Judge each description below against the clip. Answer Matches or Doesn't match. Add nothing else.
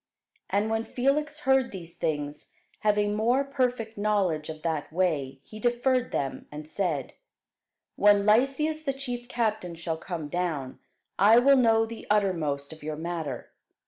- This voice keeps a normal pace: Matches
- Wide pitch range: Matches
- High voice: Matches